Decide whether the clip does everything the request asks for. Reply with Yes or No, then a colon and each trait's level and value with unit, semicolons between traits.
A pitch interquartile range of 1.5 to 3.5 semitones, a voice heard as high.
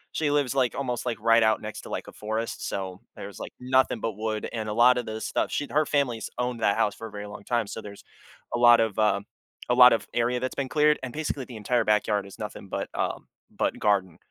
No: average, 2.9 semitones; low, 115 Hz